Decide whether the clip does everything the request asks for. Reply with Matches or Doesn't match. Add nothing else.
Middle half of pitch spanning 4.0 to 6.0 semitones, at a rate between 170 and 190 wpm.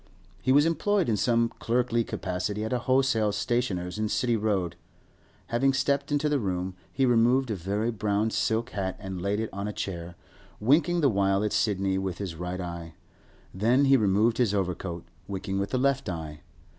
Matches